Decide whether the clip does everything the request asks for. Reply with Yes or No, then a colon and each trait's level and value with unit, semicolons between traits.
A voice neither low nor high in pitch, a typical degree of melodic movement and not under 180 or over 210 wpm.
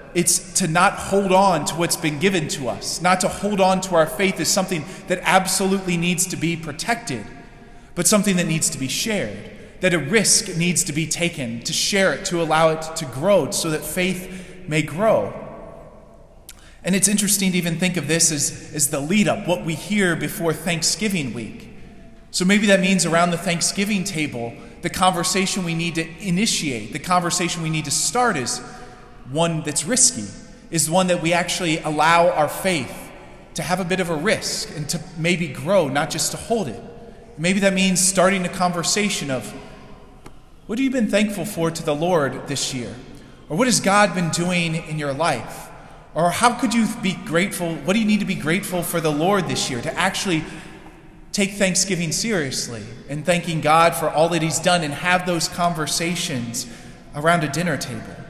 Yes: medium, 175 Hz; average, 3.1 semitones; average, 190 wpm